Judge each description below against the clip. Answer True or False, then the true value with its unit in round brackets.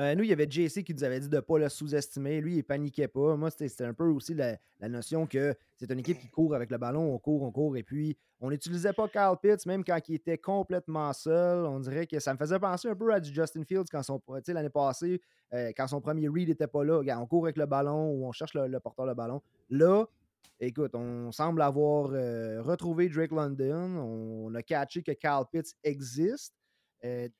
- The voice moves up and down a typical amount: True (3.6 semitones)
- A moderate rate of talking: False (240 wpm)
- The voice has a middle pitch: True (150 Hz)